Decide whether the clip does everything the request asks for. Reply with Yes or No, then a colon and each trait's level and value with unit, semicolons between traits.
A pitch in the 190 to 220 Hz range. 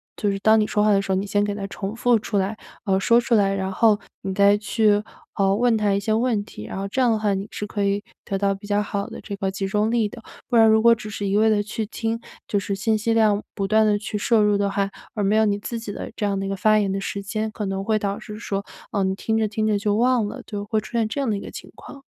Yes: high, 210 Hz